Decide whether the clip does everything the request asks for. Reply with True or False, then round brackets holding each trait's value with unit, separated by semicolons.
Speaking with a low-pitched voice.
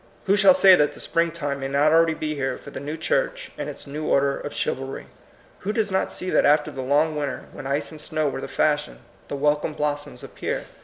False (150 Hz)